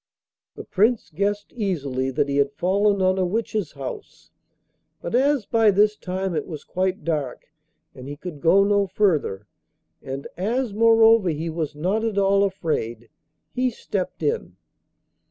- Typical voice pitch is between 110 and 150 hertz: No, high, 190 Hz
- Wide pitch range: Yes, wide, 5.8 semitones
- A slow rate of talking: No, average, 155 wpm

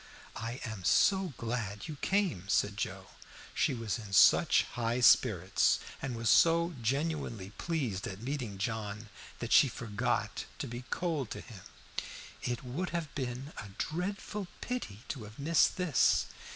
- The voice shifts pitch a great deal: Yes, wide, 6.9 semitones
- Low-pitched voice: Yes, low, 120 Hz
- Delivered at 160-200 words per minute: No, average, 150 wpm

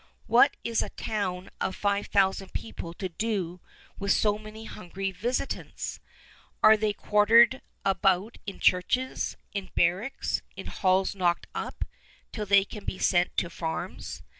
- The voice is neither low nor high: No, high, 200 Hz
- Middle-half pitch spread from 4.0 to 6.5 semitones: No, average, 2.7 semitones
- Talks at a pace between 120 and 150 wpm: Yes, average, 140 wpm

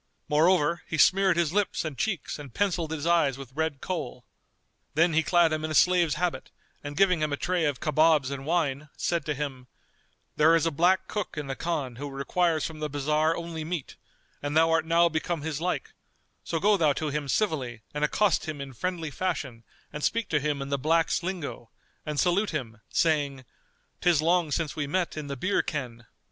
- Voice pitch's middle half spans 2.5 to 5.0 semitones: Yes, average, 3.2 semitones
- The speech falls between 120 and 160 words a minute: No, fast, 205 wpm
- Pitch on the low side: No, medium, 155 Hz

